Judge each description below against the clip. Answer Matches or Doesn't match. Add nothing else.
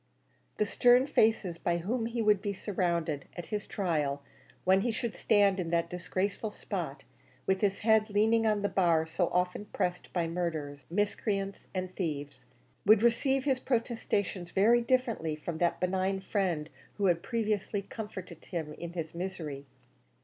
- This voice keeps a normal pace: Matches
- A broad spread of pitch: Doesn't match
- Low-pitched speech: Doesn't match